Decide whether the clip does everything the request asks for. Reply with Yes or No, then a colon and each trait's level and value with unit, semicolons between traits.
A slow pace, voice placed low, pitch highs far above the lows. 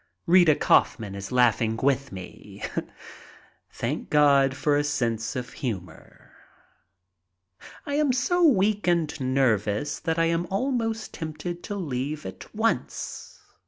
No: slow, 125 wpm; medium, 150 Hz; wide, 7.0 semitones